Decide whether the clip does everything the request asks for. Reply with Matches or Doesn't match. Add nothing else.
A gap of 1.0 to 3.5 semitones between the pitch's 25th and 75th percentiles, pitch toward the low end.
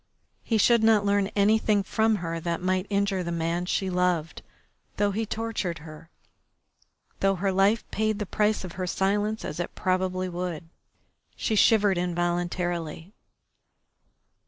Doesn't match